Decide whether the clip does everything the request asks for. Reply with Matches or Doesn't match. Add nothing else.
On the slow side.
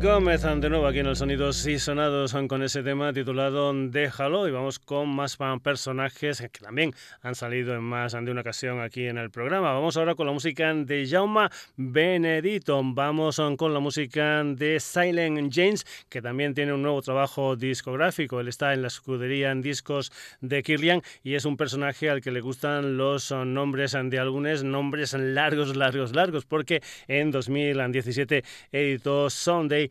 Doesn't match